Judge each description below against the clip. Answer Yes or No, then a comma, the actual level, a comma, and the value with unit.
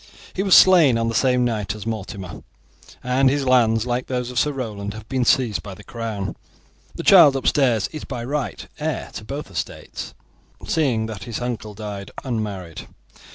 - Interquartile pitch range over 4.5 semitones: No, average, 3.6 semitones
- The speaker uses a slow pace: No, average, 175 wpm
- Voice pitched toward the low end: Yes, low, 115 Hz